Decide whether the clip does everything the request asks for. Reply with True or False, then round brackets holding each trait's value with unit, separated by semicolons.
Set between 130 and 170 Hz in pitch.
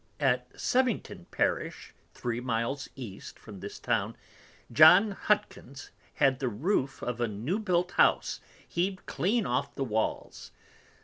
True (135 Hz)